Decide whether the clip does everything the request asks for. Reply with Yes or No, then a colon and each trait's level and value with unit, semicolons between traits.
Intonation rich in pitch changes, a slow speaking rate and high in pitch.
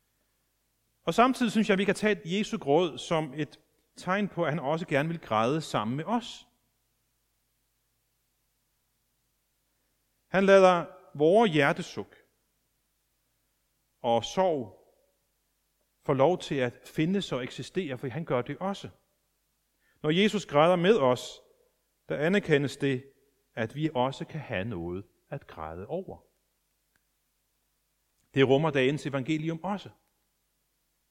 No: wide, 6.6 semitones; slow, 120 wpm; medium, 140 Hz